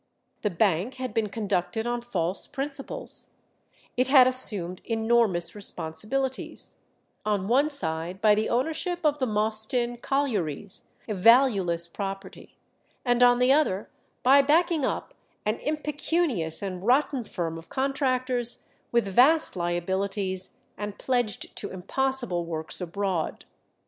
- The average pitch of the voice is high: Yes, high, 220 Hz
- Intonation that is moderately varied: No, wide, 5.8 semitones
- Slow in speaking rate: Yes, slow, 125 wpm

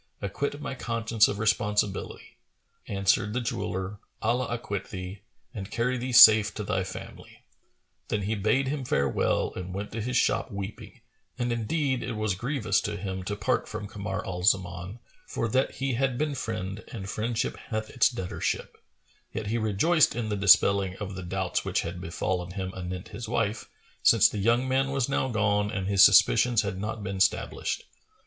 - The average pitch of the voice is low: Yes, low, 105 Hz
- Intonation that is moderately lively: Yes, average, 3.5 semitones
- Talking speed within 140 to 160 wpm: No, average, 175 wpm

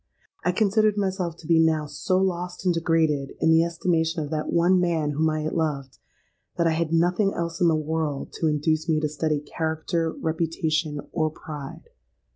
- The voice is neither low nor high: Yes, medium, 160 Hz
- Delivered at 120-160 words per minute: No, average, 185 wpm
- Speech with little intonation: Yes, narrow, 1.9 semitones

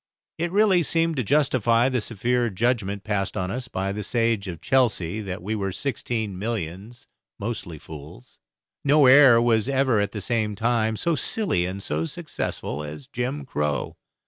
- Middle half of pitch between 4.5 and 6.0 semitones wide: Yes, average, 4.8 semitones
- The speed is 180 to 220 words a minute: No, average, 165 wpm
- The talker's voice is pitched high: No, low, 115 Hz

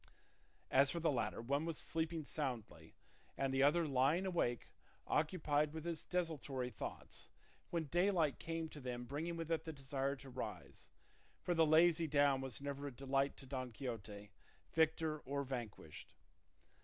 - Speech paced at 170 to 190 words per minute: No, average, 155 wpm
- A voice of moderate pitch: Yes, medium, 145 Hz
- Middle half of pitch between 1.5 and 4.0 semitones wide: Yes, average, 3.4 semitones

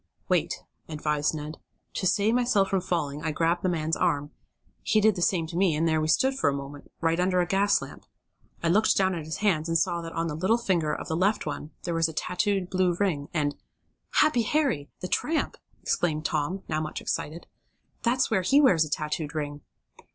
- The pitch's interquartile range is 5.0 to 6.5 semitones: No, average, 4.0 semitones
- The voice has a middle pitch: Yes, medium, 170 Hz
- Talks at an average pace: No, fast, 215 wpm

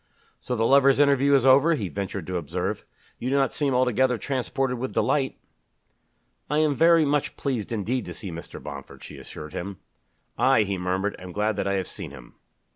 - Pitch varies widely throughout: Yes, wide, 5.8 semitones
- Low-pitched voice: Yes, low, 125 Hz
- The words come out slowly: No, average, 195 wpm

